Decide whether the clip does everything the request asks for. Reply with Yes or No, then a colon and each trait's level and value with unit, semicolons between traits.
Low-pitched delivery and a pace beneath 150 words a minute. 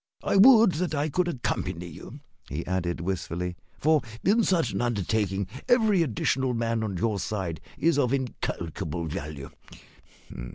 Yes: low, 115 Hz; average, 140 wpm